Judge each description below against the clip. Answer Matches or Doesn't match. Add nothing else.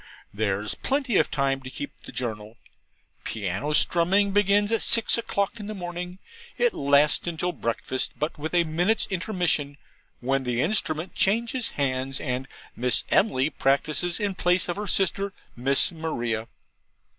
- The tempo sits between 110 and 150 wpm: Matches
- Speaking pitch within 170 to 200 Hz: Doesn't match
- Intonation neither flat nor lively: Doesn't match